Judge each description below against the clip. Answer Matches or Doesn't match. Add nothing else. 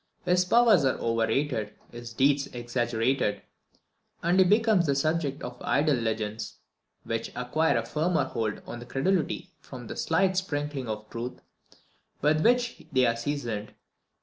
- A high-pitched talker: Doesn't match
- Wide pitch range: Matches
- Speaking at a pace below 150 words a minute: Matches